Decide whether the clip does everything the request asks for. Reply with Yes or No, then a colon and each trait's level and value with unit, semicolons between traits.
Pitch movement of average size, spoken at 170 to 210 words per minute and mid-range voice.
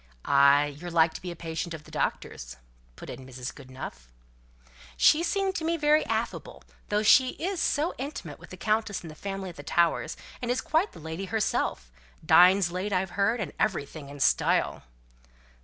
No: wide, 7.4 semitones; average, 185 wpm; medium, 180 Hz